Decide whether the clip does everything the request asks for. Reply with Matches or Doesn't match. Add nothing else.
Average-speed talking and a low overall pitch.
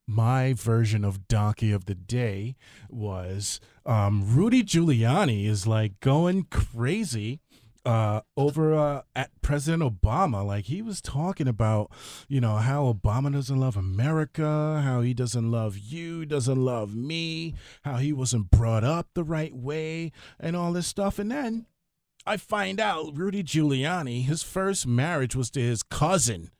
Matches